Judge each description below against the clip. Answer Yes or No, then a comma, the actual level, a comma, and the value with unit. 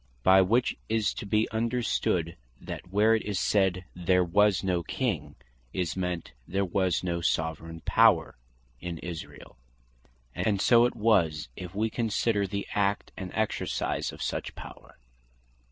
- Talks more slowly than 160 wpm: Yes, average, 145 wpm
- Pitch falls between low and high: No, very low, 95 Hz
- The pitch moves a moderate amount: Yes, average, 3.5 semitones